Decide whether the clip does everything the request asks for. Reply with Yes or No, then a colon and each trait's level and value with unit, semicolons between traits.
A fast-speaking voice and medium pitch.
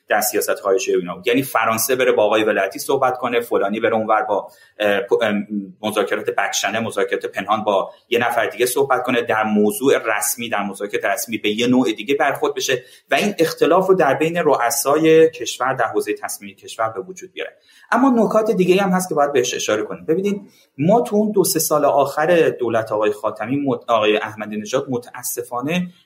Yes: fast, 180 wpm; medium, 155 Hz